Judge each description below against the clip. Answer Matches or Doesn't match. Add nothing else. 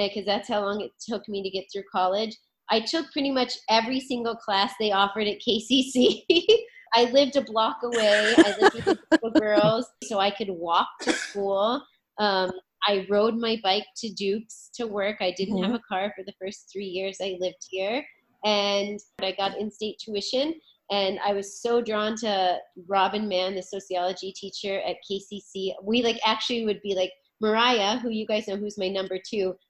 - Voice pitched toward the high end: Matches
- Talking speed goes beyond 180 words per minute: Matches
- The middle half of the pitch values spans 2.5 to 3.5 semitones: Matches